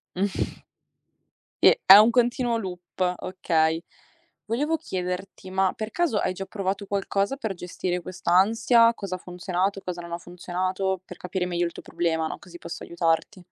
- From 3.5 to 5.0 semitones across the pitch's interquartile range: No, narrow, 2.4 semitones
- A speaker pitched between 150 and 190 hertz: Yes, medium, 185 Hz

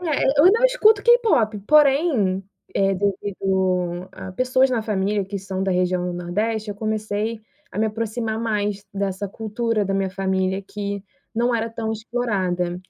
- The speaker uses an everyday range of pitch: Yes, average, 3.3 semitones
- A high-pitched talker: Yes, high, 210 Hz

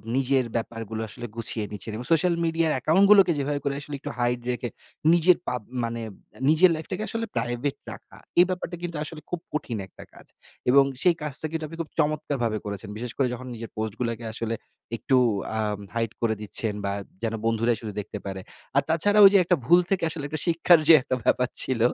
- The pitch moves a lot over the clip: Yes, wide, 6.1 semitones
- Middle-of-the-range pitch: No, low, 130 Hz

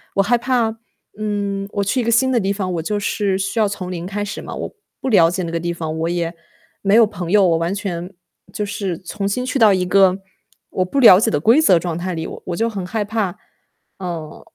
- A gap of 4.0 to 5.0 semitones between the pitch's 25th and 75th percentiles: No, average, 3.3 semitones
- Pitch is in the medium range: No, high, 195 Hz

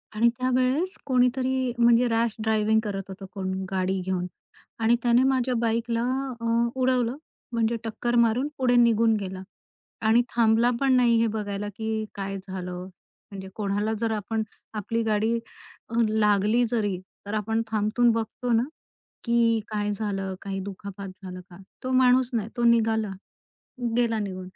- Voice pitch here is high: Yes, high, 225 Hz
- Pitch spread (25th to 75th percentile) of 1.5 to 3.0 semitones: Yes, average, 2.7 semitones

